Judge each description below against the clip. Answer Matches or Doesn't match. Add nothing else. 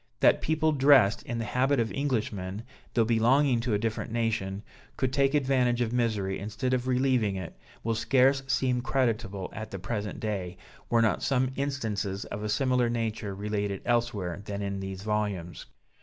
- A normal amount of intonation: Matches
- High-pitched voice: Doesn't match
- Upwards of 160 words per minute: Matches